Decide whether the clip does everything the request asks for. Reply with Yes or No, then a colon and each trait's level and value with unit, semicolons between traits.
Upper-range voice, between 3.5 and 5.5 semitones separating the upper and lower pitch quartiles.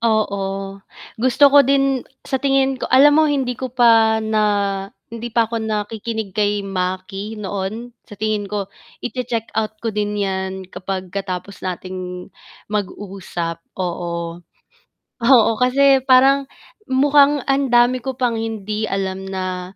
Yes: high, 215 Hz; average, 4.5 semitones